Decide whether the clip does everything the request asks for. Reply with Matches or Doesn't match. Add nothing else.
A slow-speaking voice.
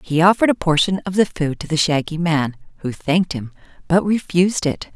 Doesn't match